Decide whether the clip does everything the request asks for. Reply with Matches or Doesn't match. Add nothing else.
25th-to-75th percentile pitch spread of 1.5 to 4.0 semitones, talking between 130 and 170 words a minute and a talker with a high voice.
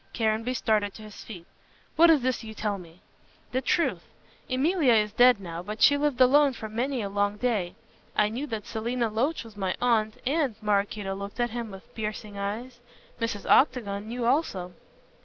Doesn't match